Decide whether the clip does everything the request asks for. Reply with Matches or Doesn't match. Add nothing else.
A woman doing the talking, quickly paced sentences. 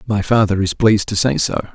Doesn't match